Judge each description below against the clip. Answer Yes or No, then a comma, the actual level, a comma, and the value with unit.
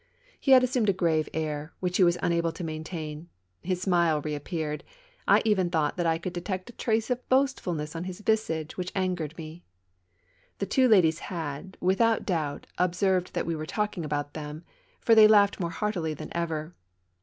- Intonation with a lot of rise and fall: No, average, 3.7 semitones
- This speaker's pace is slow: No, average, 180 wpm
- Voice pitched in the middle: Yes, medium, 175 Hz